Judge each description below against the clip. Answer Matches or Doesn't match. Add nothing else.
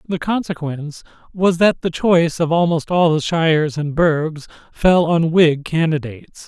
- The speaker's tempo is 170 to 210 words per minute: Doesn't match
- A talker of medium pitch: Matches